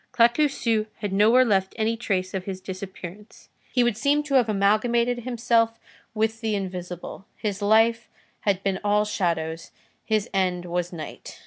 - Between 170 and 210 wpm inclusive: No, average, 150 wpm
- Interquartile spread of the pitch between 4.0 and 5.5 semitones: No, average, 3.4 semitones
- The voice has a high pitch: Yes, high, 210 Hz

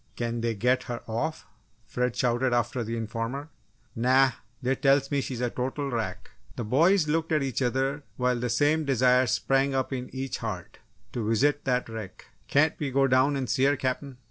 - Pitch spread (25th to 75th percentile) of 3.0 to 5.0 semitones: No, narrow, 2.5 semitones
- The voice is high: No, low, 130 Hz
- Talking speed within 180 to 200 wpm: Yes, average, 190 wpm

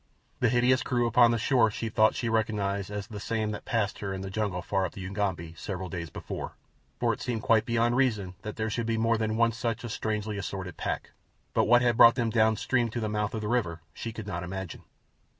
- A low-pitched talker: Yes, low, 110 Hz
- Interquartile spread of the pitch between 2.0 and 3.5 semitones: Yes, average, 2.8 semitones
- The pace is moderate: No, fast, 240 wpm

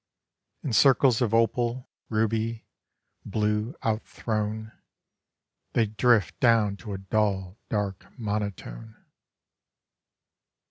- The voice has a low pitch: Yes, low, 110 Hz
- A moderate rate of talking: No, slow, 90 wpm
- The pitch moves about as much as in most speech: No, narrow, 1.9 semitones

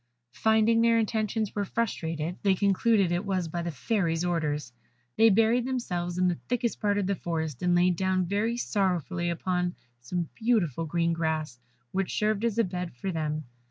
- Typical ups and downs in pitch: Yes, average, 4.3 semitones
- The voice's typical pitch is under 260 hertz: Yes, medium, 185 Hz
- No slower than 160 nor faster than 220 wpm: Yes, average, 175 wpm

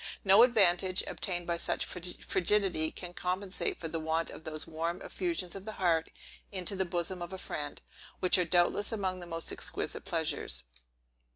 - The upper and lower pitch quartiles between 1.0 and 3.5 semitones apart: Yes, narrow, 2.4 semitones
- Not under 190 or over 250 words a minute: No, average, 170 wpm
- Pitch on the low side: No, medium, 180 Hz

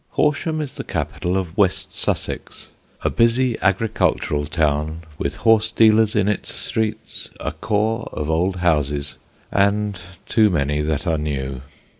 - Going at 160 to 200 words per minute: No, average, 140 wpm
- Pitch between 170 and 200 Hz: No, very low, 95 Hz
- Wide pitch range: Yes, wide, 6.4 semitones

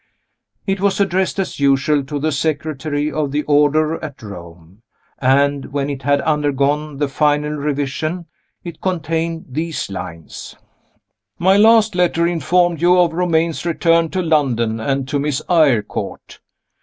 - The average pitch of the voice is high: No, medium, 150 Hz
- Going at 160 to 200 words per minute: No, average, 140 wpm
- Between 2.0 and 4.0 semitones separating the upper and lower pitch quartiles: Yes, average, 3.2 semitones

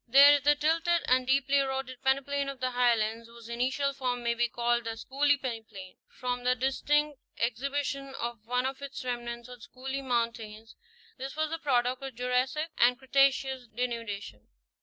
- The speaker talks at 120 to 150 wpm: No, average, 170 wpm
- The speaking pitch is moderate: No, very high, 255 Hz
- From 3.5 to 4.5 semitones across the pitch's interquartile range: No, narrow, 2.6 semitones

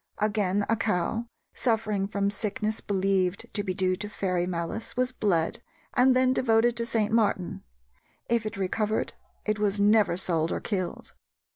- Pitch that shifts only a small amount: No, average, 3.0 semitones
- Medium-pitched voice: No, high, 210 Hz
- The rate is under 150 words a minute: No, average, 155 wpm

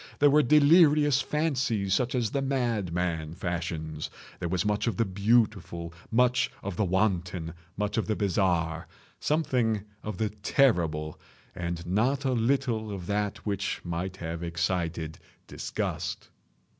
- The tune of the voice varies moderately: No, wide, 6.2 semitones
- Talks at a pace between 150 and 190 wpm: No, slow, 135 wpm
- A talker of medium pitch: No, low, 100 Hz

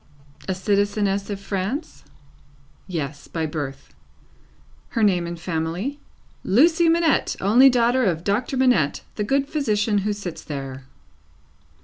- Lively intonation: Yes, wide, 6.7 semitones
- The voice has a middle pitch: No, high, 200 Hz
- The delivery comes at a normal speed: No, slow, 120 wpm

